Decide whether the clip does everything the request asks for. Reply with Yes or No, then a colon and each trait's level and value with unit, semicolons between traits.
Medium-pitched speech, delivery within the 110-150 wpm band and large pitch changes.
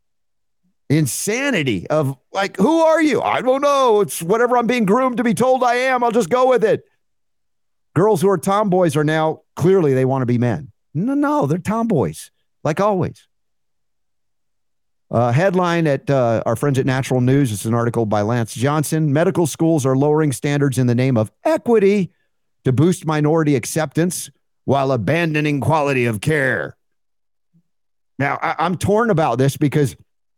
No: medium, 155 Hz; average, 165 wpm; wide, 7.4 semitones